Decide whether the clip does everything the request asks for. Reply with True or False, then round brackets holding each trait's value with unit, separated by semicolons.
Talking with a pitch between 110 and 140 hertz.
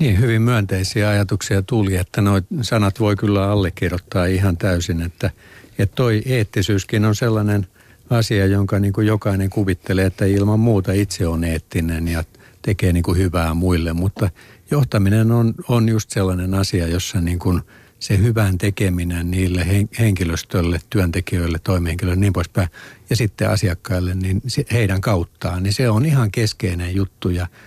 False (100 Hz)